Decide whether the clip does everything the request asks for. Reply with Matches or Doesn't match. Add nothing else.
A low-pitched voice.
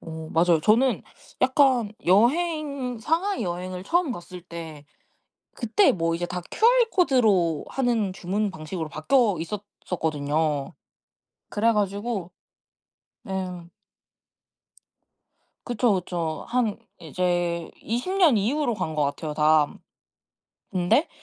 Doesn't match